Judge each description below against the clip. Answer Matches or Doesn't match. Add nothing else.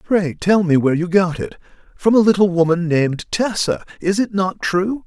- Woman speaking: Doesn't match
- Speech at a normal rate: Matches